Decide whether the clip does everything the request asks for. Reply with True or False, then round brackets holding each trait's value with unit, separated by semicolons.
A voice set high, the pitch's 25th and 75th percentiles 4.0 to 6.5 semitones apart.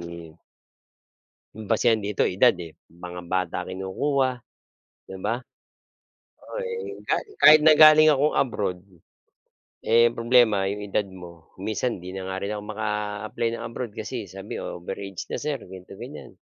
False (105 Hz; 4.4 semitones)